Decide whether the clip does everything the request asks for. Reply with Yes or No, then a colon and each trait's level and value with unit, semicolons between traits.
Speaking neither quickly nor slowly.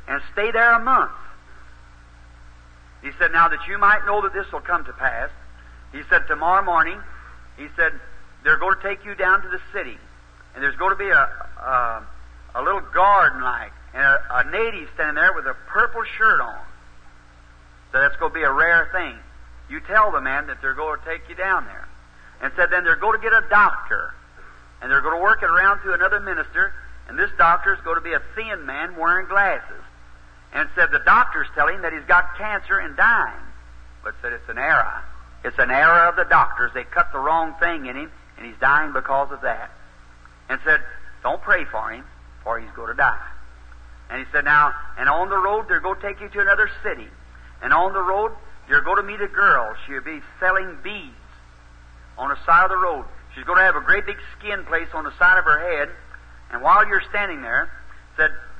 No: fast, 215 wpm